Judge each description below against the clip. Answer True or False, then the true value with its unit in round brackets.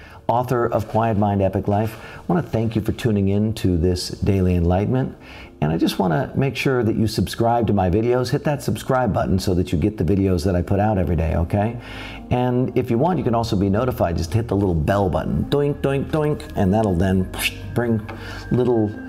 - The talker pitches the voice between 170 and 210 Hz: False (110 Hz)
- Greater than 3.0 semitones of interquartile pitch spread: True (4.1 semitones)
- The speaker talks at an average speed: False (225 wpm)